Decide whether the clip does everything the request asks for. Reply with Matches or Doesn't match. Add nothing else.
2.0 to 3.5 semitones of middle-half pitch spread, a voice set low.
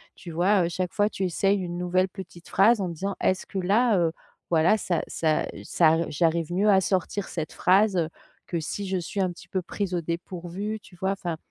Doesn't match